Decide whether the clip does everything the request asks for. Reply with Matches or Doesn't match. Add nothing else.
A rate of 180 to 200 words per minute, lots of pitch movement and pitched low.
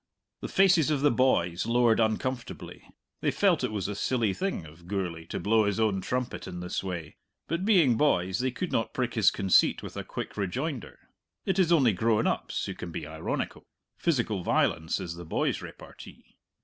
Matches